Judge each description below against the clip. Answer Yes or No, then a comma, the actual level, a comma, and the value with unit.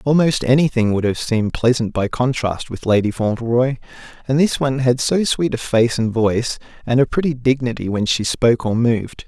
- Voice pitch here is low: Yes, low, 120 Hz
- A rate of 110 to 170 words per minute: No, average, 195 wpm